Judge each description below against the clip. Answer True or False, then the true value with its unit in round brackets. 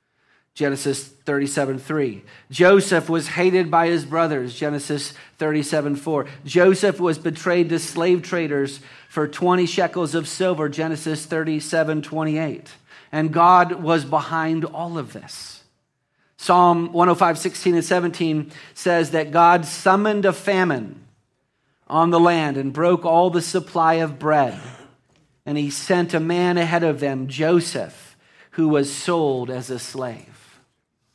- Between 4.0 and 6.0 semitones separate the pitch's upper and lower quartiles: False (3.1 semitones)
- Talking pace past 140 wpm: False (135 wpm)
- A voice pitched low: False (160 Hz)